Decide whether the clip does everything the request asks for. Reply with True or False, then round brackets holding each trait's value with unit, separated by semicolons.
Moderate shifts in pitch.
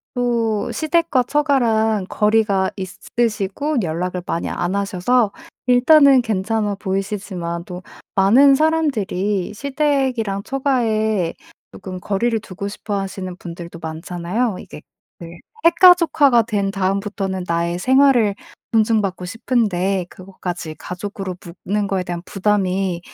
True (4.6 semitones)